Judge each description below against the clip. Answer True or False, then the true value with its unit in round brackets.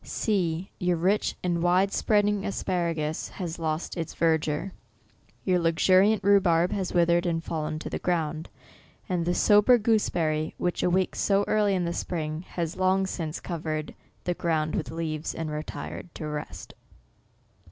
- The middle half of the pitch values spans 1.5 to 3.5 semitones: True (3.0 semitones)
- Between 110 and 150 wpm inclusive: False (165 wpm)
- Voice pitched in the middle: True (170 Hz)